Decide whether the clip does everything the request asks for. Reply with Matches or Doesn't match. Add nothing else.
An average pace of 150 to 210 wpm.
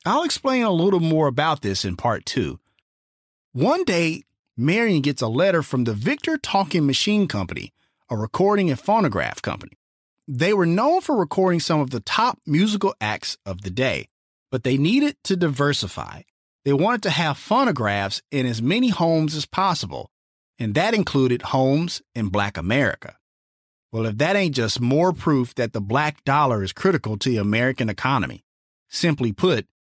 Matches